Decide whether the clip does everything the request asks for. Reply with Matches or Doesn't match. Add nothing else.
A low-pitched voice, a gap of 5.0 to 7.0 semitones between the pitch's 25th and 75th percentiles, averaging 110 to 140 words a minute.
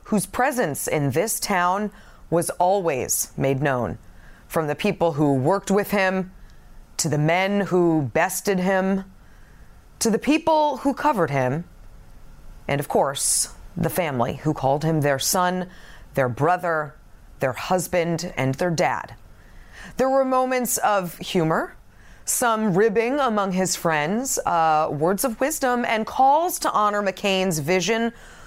Doesn't match